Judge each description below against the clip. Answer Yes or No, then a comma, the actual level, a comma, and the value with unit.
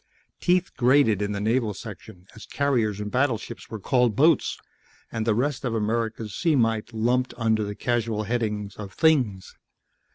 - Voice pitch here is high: No, low, 115 Hz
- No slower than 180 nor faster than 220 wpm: No, average, 160 wpm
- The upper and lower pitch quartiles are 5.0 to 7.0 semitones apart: No, average, 3.1 semitones